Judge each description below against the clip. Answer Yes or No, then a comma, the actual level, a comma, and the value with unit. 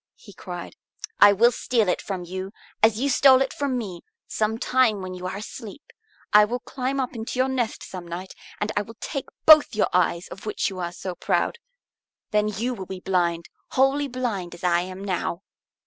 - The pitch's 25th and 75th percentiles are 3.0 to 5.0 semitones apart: No, wide, 5.4 semitones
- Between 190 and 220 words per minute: Yes, average, 200 wpm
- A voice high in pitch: Yes, high, 210 Hz